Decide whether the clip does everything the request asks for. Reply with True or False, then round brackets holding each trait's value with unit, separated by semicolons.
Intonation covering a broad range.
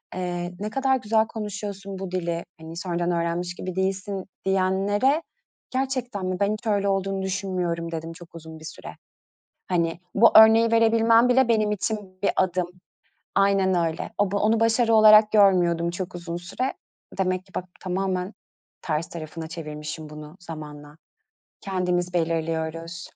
False (3.6 semitones)